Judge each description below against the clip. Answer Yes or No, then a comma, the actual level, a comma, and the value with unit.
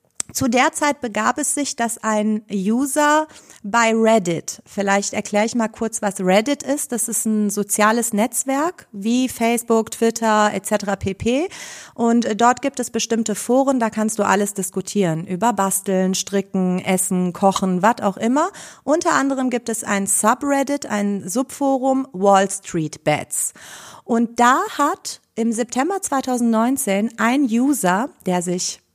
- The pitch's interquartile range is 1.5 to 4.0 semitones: No, average, 4.4 semitones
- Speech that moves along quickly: No, average, 145 wpm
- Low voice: No, high, 225 Hz